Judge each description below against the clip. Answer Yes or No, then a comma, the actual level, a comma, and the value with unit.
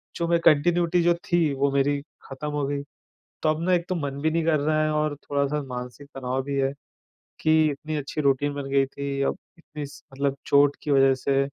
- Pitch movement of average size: No, narrow, 2.1 semitones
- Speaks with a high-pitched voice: No, medium, 145 Hz